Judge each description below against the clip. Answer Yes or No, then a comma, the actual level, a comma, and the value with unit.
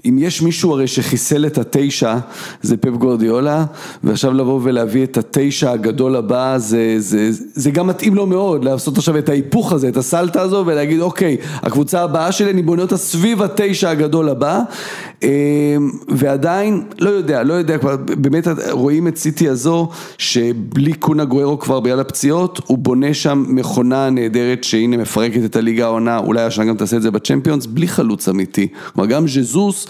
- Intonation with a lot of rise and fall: No, average, 5.0 semitones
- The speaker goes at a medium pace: No, fast, 170 wpm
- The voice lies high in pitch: No, medium, 140 Hz